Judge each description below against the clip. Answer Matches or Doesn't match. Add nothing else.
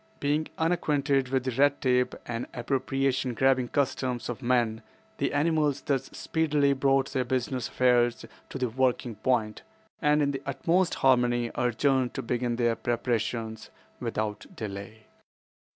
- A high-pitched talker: Doesn't match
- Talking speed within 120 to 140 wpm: Matches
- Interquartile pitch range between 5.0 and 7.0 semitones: Doesn't match